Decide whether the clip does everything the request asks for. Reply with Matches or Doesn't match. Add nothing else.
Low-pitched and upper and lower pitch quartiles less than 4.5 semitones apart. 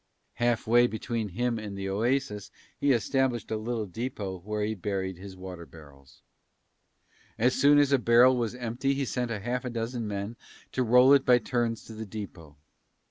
Matches